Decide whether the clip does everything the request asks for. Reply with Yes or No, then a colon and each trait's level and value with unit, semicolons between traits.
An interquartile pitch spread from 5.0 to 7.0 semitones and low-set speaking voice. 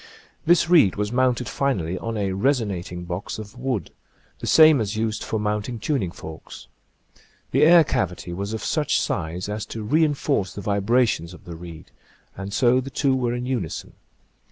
Yes: average, 5.3 semitones; low, 110 Hz